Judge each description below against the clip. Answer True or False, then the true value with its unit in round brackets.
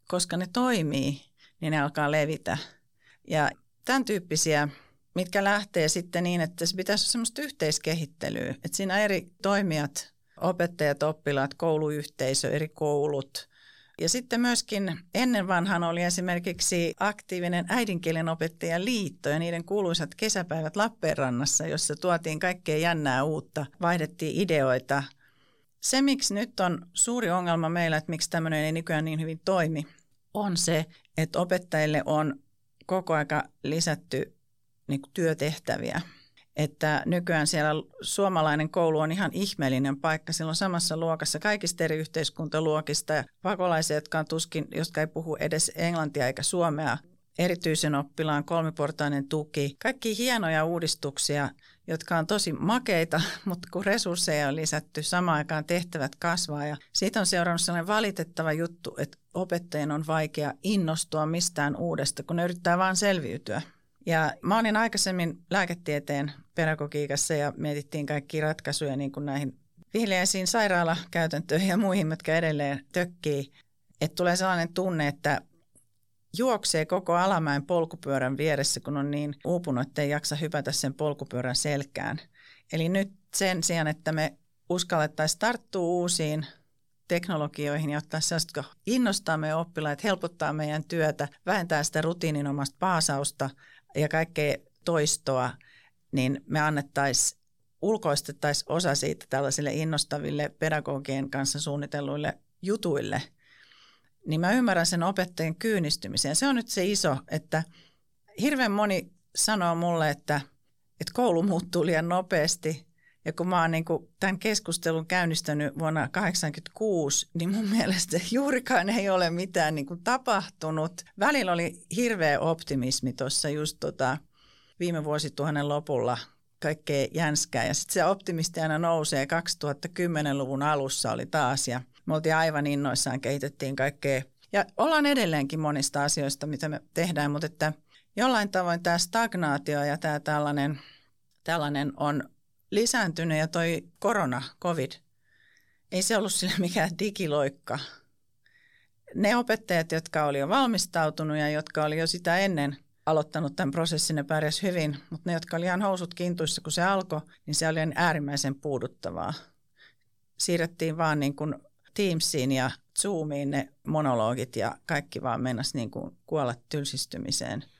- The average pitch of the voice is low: False (160 Hz)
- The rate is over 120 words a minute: True (130 wpm)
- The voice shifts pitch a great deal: False (3.4 semitones)